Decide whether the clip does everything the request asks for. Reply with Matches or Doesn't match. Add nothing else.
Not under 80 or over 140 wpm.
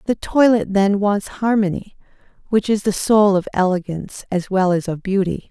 Doesn't match